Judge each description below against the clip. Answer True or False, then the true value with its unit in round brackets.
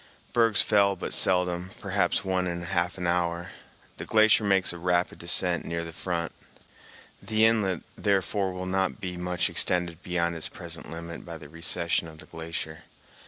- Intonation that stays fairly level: True (2.0 semitones)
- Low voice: True (90 Hz)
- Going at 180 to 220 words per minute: False (165 wpm)